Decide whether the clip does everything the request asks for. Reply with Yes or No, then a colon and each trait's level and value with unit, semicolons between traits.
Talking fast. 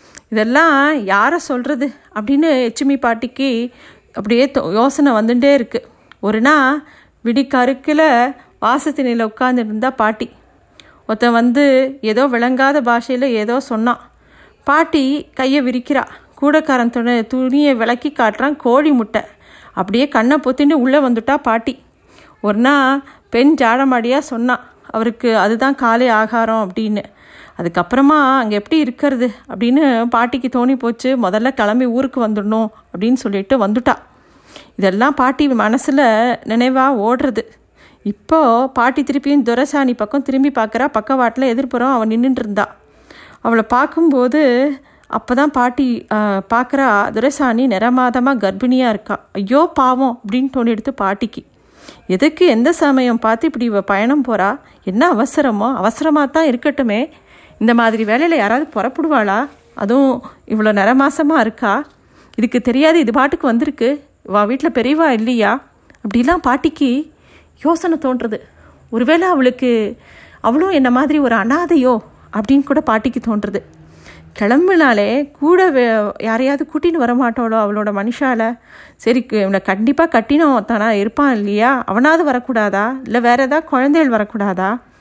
No: average, 115 wpm